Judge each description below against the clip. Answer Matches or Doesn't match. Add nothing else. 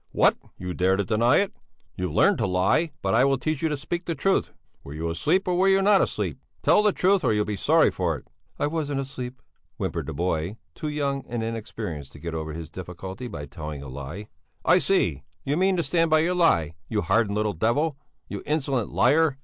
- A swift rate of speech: Matches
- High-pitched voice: Doesn't match